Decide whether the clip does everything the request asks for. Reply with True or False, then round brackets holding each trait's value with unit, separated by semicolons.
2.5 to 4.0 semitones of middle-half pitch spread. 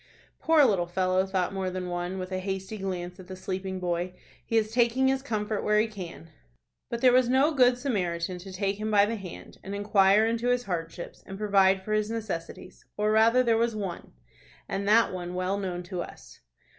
True (3.4 semitones)